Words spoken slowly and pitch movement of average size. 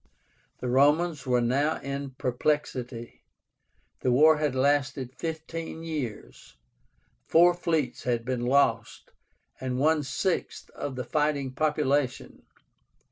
Yes: slow, 110 wpm; average, 3.3 semitones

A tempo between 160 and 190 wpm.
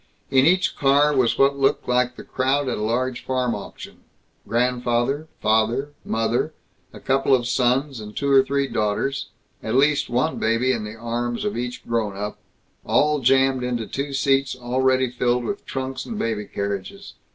Yes: average, 170 wpm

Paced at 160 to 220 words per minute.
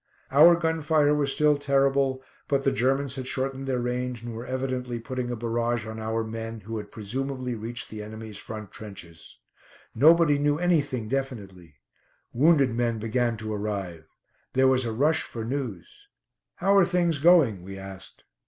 Yes: average, 165 wpm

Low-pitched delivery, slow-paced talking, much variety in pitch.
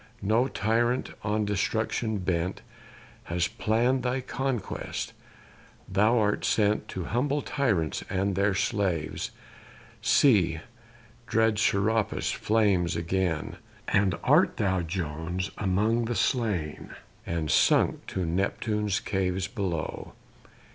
No: low, 100 Hz; slow, 105 wpm; average, 3.5 semitones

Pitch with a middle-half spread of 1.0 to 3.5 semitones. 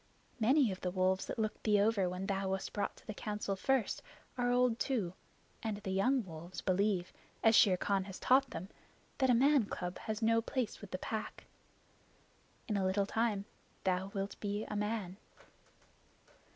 Yes: average, 3.2 semitones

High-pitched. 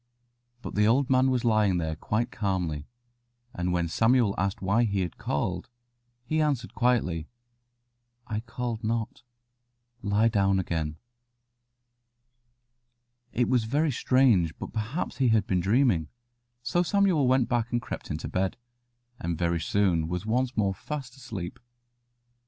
No: low, 110 Hz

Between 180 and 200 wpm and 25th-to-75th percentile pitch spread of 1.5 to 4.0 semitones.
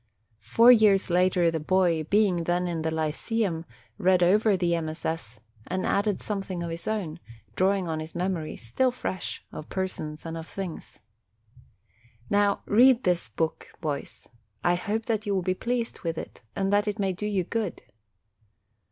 No: average, 170 wpm; average, 3.7 semitones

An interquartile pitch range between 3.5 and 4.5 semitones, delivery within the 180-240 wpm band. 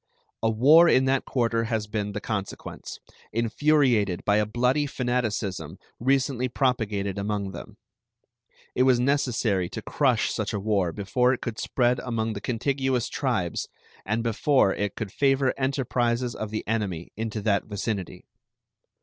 No: average, 3.8 semitones; average, 145 wpm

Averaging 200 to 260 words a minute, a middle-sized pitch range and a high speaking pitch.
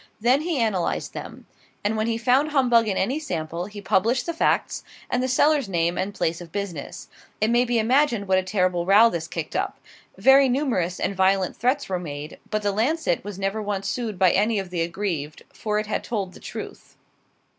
Yes: fast, 205 wpm; average, 4.9 semitones; high, 205 Hz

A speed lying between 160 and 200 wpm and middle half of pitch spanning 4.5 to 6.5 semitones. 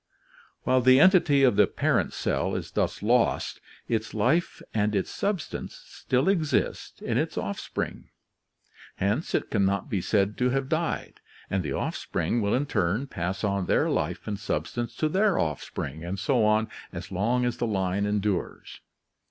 Yes: average, 165 wpm; average, 5.3 semitones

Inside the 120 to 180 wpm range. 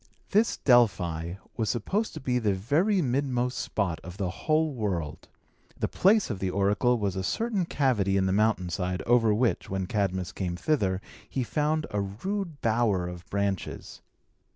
Yes: average, 165 wpm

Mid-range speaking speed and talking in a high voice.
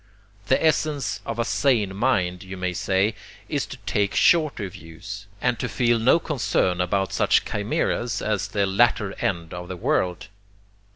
No: average, 160 wpm; low, 100 Hz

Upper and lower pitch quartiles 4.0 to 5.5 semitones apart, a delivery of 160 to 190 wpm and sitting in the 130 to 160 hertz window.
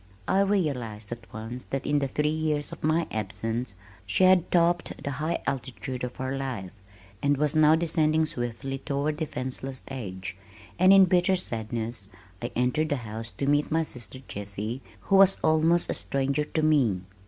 Yes: average, 4.7 semitones; average, 170 wpm; medium, 140 Hz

